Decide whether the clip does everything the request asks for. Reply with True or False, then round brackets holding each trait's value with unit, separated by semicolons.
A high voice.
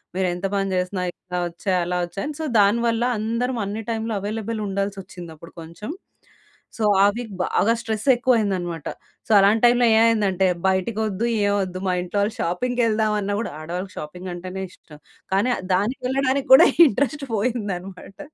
True (205 Hz)